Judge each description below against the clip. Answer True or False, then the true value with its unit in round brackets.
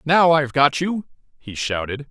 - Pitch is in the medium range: True (145 Hz)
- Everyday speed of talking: True (170 wpm)